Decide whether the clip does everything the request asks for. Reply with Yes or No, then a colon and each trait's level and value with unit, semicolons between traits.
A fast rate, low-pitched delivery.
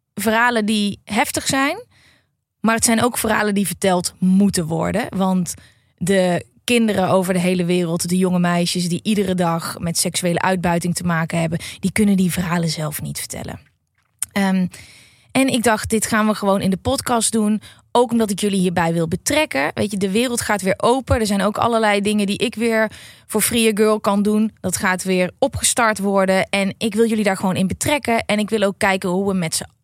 No: fast, 205 wpm; high, 195 Hz